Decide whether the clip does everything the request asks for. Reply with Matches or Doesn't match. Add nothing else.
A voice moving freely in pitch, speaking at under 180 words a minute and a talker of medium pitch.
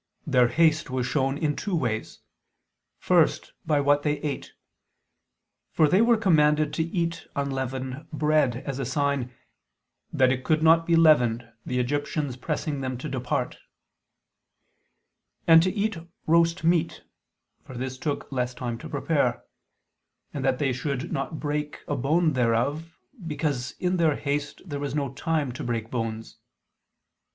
Doesn't match